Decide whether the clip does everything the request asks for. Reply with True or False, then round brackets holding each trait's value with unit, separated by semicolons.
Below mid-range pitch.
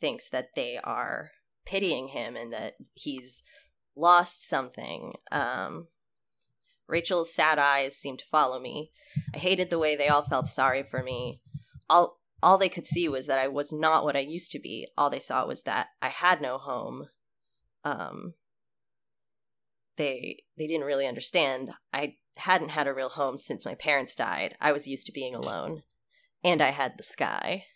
False (145 Hz)